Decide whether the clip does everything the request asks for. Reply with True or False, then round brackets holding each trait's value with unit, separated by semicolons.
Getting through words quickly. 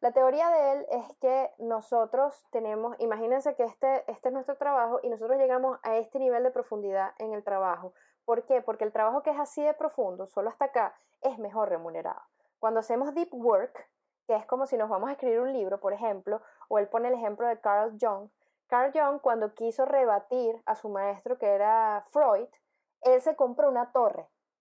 True (200 wpm)